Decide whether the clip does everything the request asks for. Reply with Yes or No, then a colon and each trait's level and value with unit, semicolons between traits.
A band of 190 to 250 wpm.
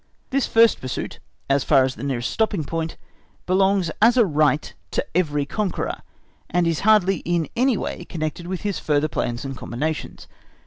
No: average, 170 wpm